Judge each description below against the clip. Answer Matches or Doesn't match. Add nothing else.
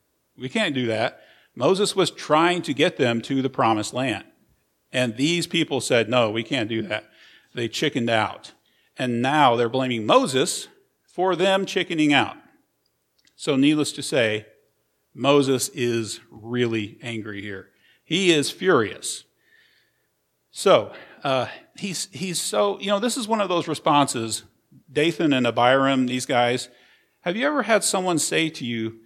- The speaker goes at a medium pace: Matches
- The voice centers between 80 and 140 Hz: Matches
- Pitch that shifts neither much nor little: Doesn't match